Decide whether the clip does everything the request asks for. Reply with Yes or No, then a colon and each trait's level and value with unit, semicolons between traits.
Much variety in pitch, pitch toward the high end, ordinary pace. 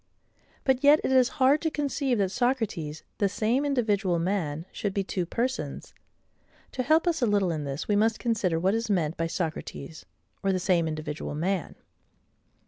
Yes: wide, 7.1 semitones; high, 200 Hz; average, 175 wpm